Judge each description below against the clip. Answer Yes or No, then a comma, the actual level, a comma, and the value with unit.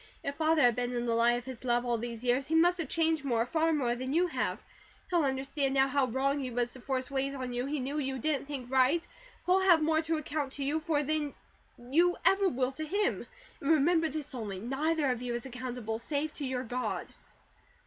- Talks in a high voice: Yes, very high, 275 Hz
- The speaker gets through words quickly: Yes, fast, 230 wpm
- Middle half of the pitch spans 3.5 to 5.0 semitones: Yes, average, 3.9 semitones